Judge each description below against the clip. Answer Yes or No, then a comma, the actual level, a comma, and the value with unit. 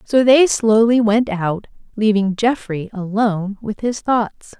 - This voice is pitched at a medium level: No, high, 215 Hz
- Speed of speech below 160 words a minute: Yes, average, 145 wpm